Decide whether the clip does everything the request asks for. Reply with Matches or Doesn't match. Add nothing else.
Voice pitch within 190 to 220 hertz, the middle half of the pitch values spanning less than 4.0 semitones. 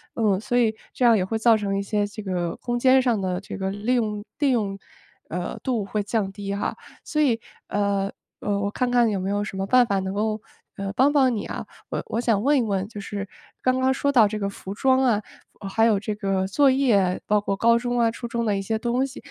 Matches